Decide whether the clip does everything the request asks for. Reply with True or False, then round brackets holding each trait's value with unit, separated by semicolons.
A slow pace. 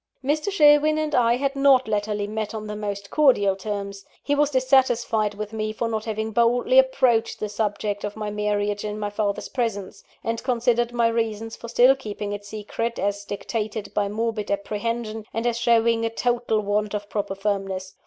False (185 wpm)